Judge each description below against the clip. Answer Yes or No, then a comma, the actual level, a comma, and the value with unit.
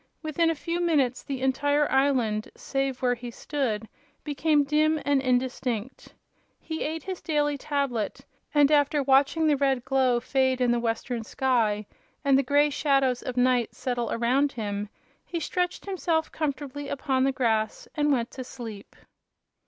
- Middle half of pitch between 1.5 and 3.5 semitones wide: Yes, average, 3.1 semitones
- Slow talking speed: No, average, 155 wpm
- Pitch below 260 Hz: No, very high, 270 Hz